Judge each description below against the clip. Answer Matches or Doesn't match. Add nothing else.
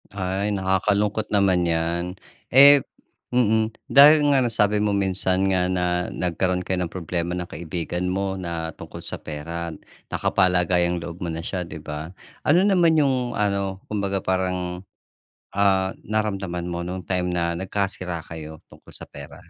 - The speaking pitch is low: Matches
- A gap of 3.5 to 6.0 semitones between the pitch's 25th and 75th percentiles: Doesn't match